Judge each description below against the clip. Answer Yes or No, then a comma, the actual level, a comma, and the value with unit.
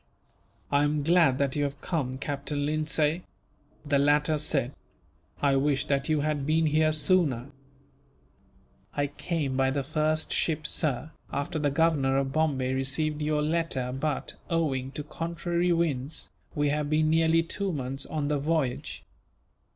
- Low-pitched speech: No, medium, 150 Hz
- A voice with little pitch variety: Yes, narrow, 2.3 semitones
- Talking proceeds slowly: No, average, 150 wpm